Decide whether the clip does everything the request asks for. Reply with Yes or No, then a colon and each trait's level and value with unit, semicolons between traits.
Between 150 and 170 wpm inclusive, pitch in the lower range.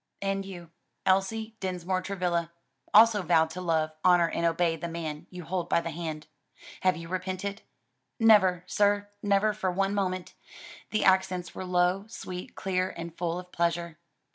No: average, 160 wpm; medium, 180 Hz